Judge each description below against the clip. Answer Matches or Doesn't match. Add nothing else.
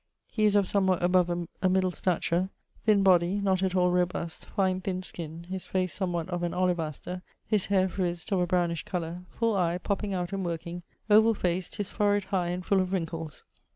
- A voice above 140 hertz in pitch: Matches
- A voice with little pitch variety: Matches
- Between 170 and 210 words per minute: Matches